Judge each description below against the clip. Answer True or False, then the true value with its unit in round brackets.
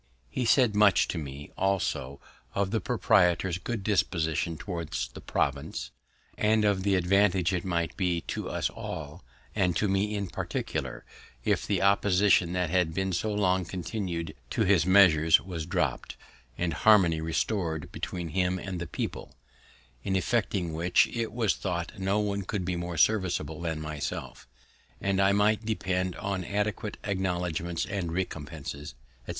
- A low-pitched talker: True (95 Hz)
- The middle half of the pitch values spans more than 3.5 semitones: False (3.0 semitones)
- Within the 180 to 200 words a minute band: False (155 wpm)